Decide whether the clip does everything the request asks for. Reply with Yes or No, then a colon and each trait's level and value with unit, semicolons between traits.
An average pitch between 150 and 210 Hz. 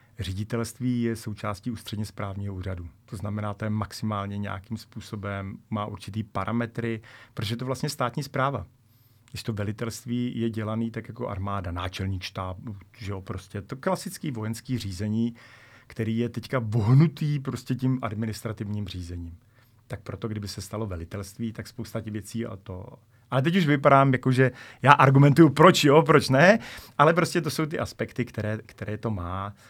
No: low, 115 Hz